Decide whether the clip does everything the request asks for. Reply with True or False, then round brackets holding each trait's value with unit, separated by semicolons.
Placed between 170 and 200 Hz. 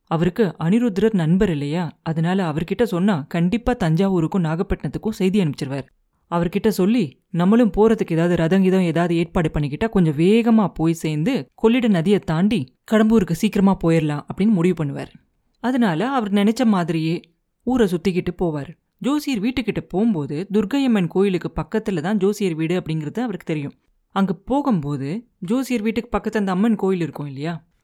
True (185 Hz)